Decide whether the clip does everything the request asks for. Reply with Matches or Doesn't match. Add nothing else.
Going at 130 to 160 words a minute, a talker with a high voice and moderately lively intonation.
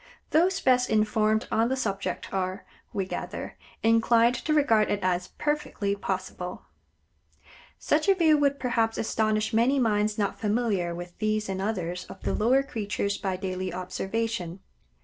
Matches